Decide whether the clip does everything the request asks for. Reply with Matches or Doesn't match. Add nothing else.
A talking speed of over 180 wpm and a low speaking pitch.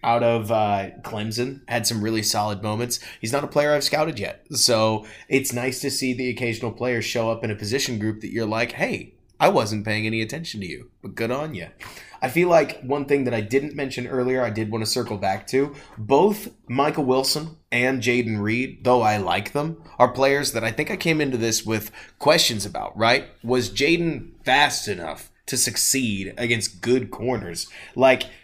Matches